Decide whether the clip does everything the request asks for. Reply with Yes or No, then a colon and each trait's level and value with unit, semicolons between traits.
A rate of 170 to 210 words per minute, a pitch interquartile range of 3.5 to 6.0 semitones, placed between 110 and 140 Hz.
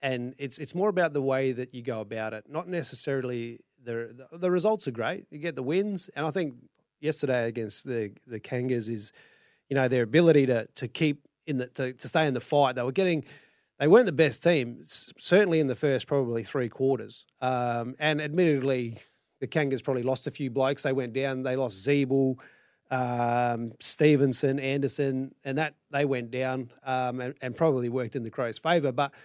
No: average, 200 wpm; average, 3.1 semitones; low, 135 Hz